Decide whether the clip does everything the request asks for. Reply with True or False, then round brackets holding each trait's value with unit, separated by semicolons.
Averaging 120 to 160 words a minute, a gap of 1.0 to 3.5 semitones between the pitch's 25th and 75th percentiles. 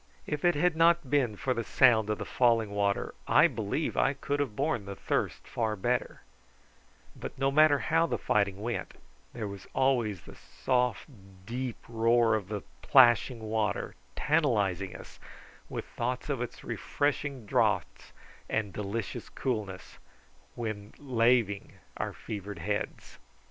False (145 wpm; 4.3 semitones)